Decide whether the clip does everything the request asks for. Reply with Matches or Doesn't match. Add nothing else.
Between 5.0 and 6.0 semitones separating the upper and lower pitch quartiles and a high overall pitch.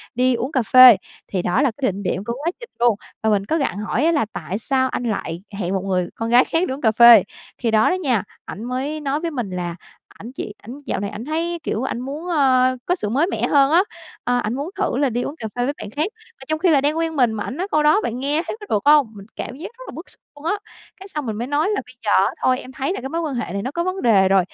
Matches